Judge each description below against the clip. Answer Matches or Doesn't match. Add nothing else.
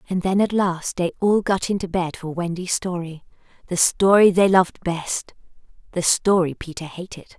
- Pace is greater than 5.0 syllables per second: Doesn't match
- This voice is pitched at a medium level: Matches